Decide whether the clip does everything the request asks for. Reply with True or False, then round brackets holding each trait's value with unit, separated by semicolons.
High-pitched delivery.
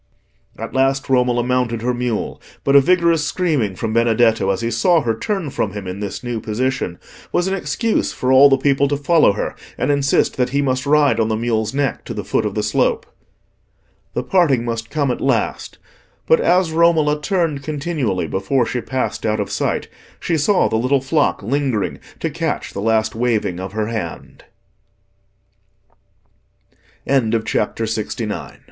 False (125 Hz)